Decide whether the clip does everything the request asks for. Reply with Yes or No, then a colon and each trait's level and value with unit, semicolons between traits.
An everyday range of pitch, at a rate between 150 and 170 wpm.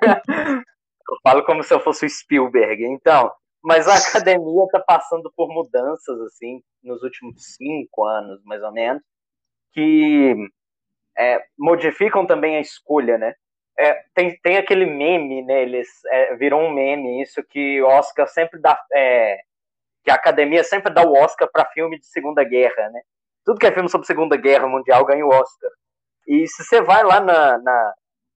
No: wide, 5.9 semitones; average, 165 wpm